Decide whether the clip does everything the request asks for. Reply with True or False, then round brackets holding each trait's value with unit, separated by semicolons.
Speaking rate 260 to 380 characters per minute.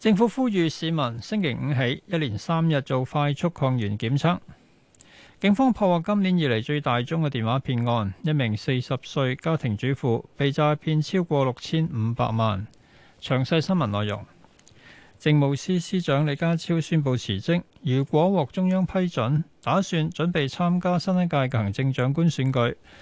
False (250 characters per minute)